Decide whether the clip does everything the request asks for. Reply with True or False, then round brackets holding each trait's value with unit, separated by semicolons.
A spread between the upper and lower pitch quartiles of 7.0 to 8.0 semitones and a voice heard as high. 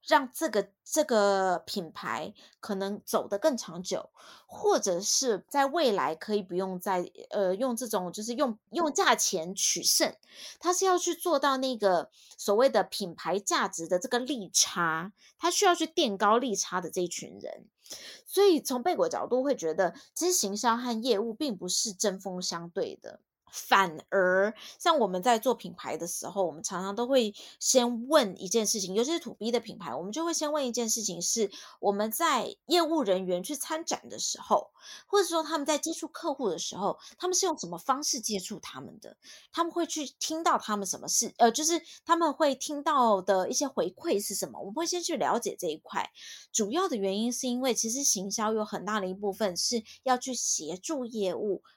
True (7.6 semitones; 230 Hz)